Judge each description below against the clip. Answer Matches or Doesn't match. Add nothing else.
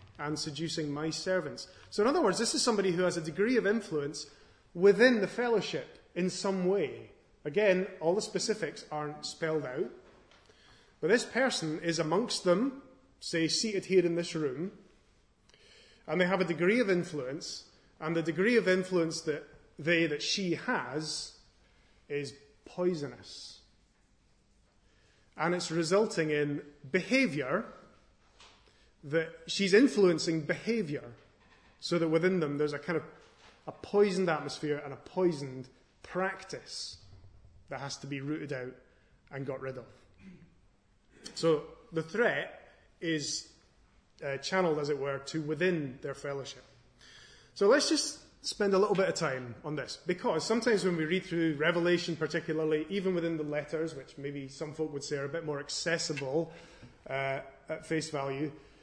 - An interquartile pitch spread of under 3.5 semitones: Doesn't match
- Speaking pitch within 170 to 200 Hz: Doesn't match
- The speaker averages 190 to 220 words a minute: Doesn't match